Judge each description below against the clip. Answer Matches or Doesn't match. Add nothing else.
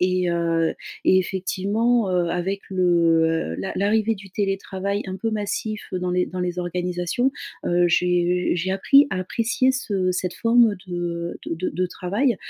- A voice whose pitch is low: Doesn't match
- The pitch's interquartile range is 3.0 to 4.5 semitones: Doesn't match